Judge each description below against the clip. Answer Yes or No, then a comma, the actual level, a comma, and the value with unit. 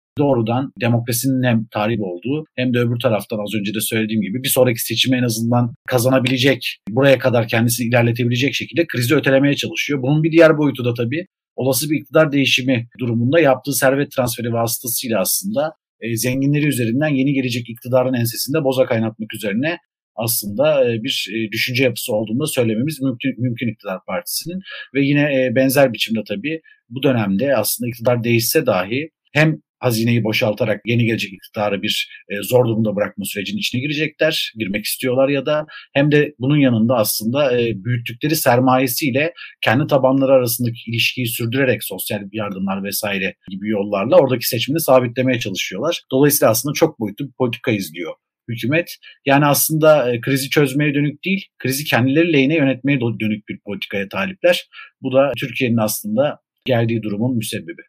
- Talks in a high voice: No, low, 125 Hz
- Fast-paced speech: Yes, fast, 150 wpm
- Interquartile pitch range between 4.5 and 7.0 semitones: No, average, 3.5 semitones